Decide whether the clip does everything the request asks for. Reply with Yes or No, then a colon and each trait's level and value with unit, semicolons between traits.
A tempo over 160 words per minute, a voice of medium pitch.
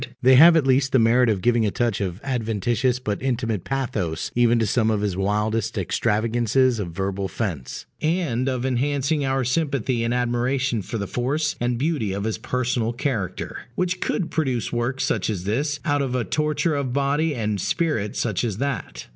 No: average, 185 wpm; low, 120 Hz